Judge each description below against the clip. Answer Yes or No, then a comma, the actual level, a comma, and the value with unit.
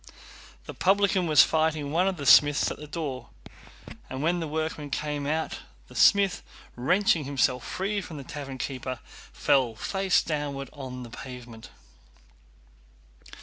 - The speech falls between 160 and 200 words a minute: No, average, 145 wpm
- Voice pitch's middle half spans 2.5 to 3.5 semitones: No, average, 4.0 semitones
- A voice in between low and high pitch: Yes, medium, 145 Hz